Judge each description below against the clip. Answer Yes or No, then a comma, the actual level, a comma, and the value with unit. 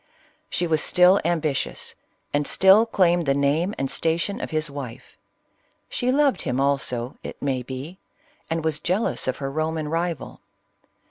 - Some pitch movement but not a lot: Yes, average, 4.1 semitones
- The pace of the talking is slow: No, average, 150 wpm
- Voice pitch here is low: No, medium, 160 Hz